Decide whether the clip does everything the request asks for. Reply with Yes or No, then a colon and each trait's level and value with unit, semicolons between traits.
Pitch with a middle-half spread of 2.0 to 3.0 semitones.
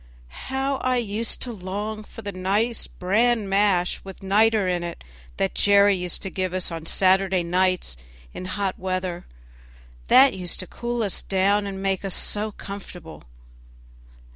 Yes: narrow, 2.5 semitones